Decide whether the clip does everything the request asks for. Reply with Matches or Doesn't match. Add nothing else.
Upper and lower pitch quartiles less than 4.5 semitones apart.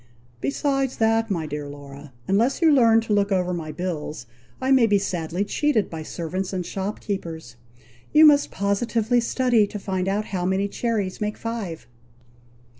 Doesn't match